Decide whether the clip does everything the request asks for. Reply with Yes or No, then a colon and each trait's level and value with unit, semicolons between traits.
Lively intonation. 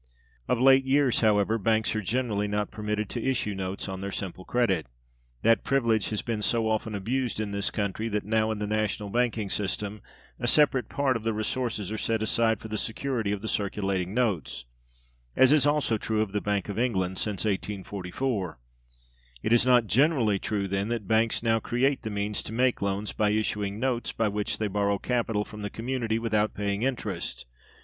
No: narrow, 2.6 semitones